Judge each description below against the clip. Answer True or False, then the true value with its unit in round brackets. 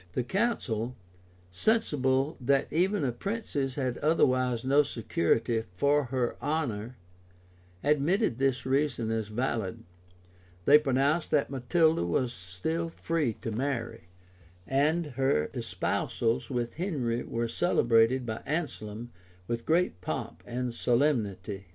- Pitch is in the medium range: False (130 Hz)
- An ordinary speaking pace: False (115 wpm)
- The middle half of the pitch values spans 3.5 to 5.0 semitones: True (4.3 semitones)